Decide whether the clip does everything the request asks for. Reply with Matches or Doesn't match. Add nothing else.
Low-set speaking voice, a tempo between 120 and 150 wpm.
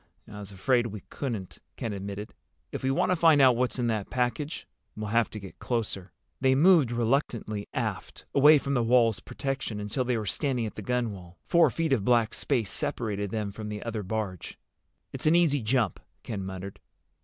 Doesn't match